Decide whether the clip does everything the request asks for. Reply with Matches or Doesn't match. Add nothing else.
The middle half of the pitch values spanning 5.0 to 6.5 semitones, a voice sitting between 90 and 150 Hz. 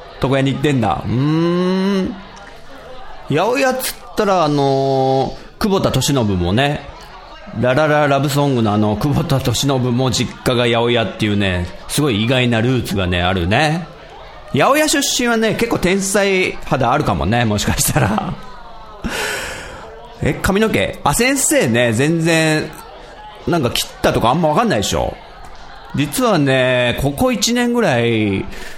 Doesn't match